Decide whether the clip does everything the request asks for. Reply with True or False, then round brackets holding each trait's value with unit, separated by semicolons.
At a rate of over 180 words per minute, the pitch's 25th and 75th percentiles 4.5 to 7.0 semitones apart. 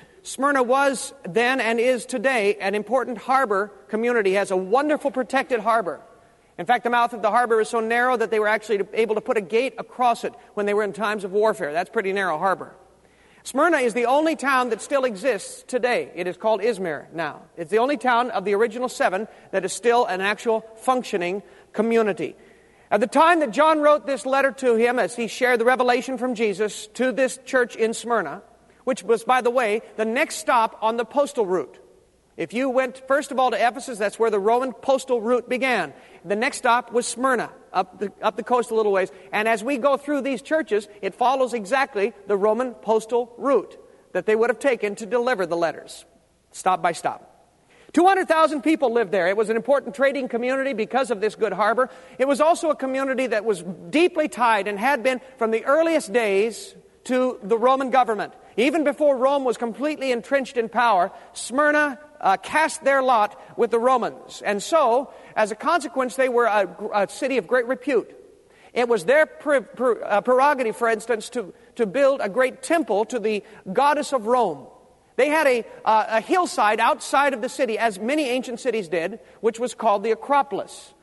False (200 wpm; 3.5 semitones)